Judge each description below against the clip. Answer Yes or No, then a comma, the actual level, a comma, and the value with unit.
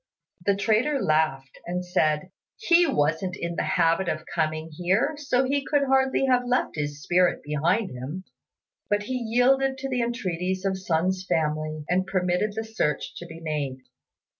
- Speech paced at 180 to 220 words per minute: No, average, 165 wpm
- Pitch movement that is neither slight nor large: No, wide, 7.6 semitones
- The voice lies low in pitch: No, medium, 185 Hz